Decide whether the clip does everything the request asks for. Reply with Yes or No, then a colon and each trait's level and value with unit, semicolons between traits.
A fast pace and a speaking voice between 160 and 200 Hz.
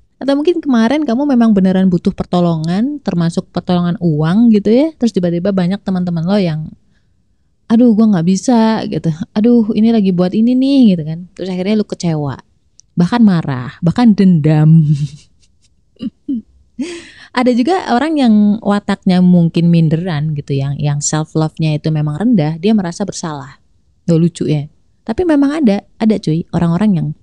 Yes: fast, 150 wpm; medium, 185 Hz